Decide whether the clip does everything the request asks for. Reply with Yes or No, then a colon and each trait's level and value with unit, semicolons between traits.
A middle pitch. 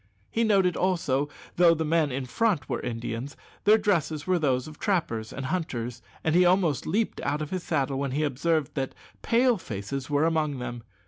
Yes: medium, 155 Hz